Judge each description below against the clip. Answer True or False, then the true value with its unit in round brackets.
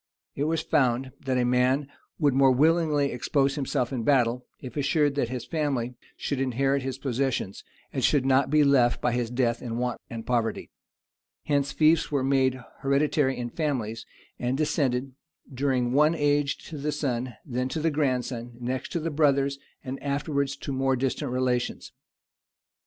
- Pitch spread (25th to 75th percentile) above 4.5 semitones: False (2.6 semitones)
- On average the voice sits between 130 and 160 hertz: True (135 Hz)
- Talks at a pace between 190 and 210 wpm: False (165 wpm)